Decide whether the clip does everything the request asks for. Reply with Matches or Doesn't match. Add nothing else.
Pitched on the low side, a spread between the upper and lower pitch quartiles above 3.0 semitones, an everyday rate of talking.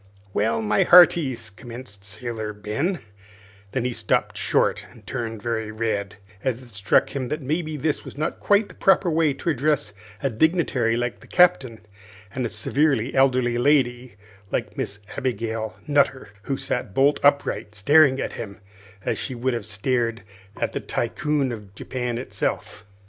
Matches